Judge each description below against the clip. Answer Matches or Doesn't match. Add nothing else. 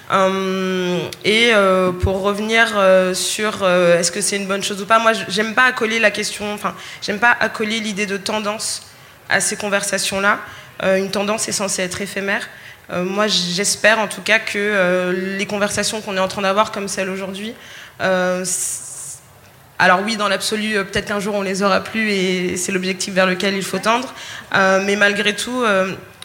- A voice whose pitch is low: Doesn't match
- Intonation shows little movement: Matches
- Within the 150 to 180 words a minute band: Doesn't match